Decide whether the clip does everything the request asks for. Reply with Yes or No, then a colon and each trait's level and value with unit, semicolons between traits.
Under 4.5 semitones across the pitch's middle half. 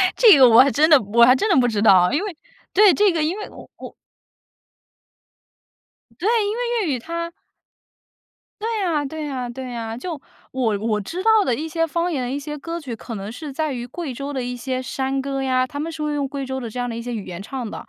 No: average, 5.2 semitones